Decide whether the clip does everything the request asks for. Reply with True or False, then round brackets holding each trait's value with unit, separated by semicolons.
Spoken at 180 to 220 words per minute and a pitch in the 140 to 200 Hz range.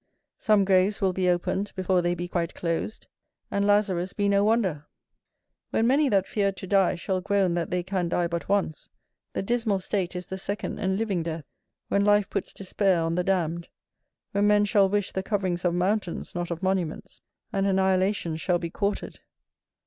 True (185 wpm; 190 Hz)